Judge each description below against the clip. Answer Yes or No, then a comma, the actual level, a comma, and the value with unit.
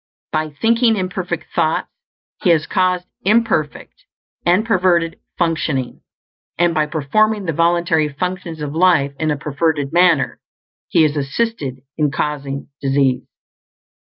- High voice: No, medium, 165 Hz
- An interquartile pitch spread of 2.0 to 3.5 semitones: No, average, 4.0 semitones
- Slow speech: Yes, slow, 125 wpm